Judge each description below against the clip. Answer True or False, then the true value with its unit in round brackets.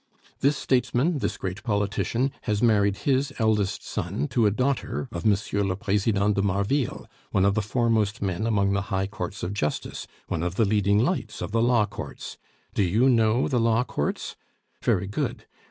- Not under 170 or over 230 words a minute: True (180 wpm)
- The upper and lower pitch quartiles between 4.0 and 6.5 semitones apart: False (3.2 semitones)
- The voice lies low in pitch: True (105 Hz)